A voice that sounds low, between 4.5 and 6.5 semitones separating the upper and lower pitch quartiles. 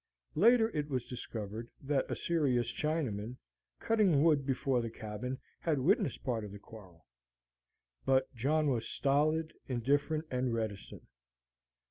Yes: low, 130 Hz; average, 4.9 semitones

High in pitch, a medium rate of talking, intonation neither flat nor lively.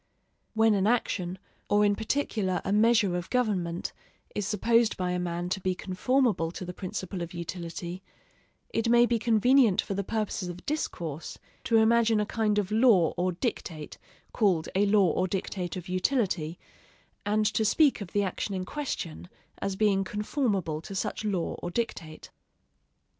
Yes: high, 200 Hz; average, 165 wpm; average, 3.7 semitones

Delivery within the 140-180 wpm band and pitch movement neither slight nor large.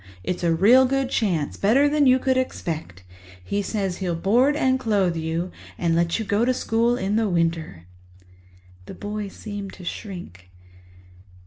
No: average, 155 wpm; wide, 6.1 semitones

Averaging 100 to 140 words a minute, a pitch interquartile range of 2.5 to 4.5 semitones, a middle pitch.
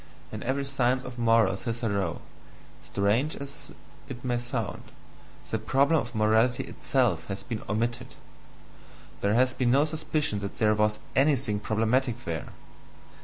No: slow, 135 wpm; average, 3.7 semitones; low, 120 Hz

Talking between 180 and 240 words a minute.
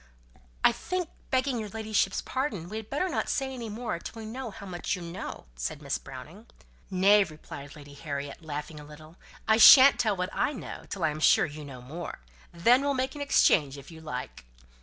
Yes: fast, 205 wpm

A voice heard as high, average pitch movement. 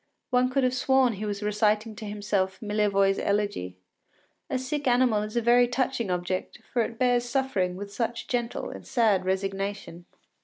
Yes: high, 215 Hz; average, 3.8 semitones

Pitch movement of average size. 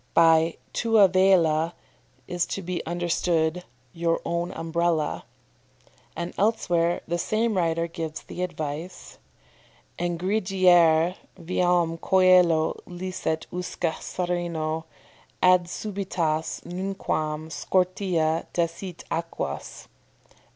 No: narrow, 2.0 semitones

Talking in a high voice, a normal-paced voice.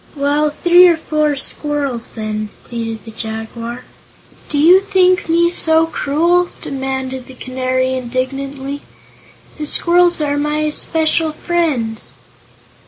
No: very high, 285 Hz; slow, 115 wpm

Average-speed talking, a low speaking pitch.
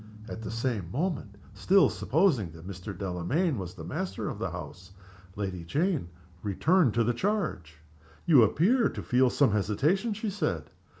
Yes: average, 160 wpm; low, 115 Hz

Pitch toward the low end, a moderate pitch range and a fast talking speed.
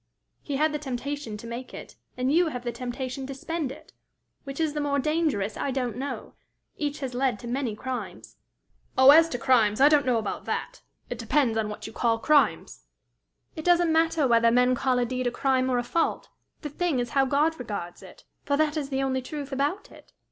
No: very high, 265 Hz; average, 3.3 semitones; fast, 215 wpm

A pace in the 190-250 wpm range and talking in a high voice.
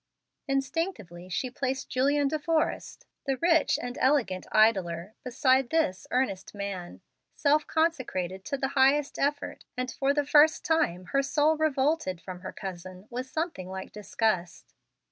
No: average, 145 wpm; very high, 260 Hz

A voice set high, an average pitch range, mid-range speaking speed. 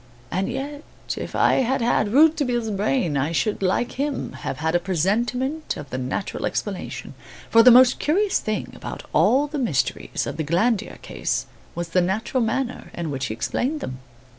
No: high, 220 Hz; wide, 7.4 semitones; average, 175 wpm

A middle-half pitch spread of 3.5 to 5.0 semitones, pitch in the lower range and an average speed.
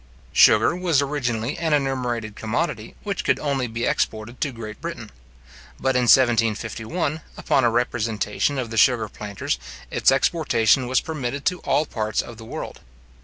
Yes: average, 4.2 semitones; low, 125 Hz; average, 155 wpm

